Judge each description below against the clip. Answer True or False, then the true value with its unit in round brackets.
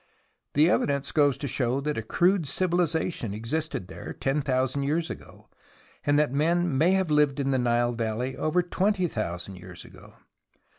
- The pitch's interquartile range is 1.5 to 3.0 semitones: False (5.0 semitones)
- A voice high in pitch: False (140 Hz)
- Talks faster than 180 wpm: False (170 wpm)